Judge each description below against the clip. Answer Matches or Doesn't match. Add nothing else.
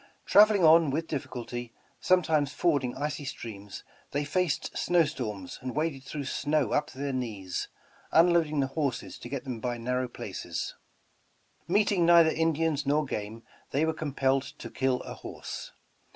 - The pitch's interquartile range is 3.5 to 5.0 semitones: Matches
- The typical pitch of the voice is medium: Matches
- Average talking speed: Matches